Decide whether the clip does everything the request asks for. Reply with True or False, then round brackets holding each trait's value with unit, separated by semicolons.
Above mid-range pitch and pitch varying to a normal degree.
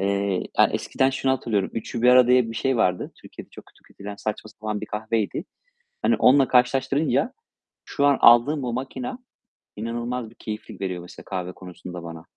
False (115 Hz; 4.6 semitones)